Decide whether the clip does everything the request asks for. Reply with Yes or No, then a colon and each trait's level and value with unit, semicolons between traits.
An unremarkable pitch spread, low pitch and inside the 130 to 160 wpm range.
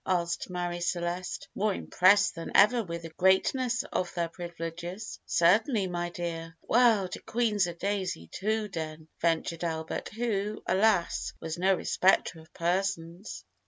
No: average, 3.2 semitones; medium, 180 Hz; average, 140 wpm